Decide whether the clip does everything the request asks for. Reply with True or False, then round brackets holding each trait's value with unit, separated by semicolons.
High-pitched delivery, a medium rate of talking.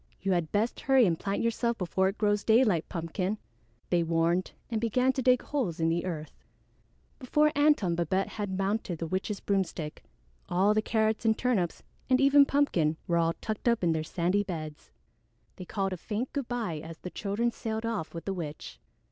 True (195 Hz; 190 wpm)